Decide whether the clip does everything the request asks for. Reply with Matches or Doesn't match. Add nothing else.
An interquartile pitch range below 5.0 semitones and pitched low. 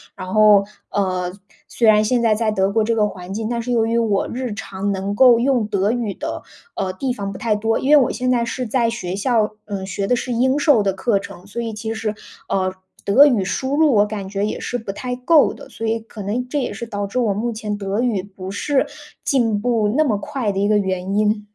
Doesn't match